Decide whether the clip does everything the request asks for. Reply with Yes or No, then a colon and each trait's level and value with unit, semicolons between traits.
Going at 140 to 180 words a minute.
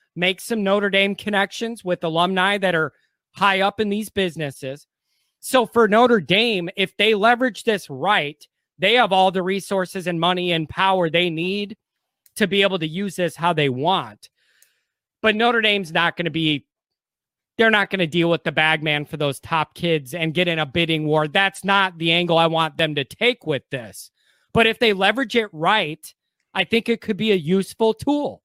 No: average, 195 wpm